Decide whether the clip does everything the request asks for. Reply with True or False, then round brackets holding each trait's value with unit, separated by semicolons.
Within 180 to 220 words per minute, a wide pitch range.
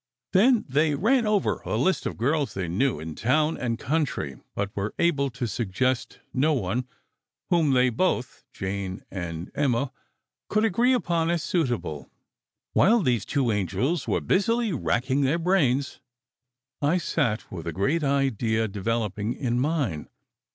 False (150 wpm; 7.2 semitones)